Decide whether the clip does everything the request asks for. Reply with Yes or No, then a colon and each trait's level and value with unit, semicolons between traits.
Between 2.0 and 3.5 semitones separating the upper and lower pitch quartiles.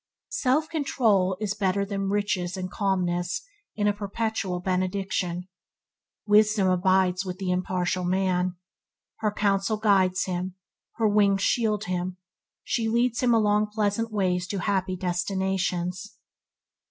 Yes: narrow, 2.5 semitones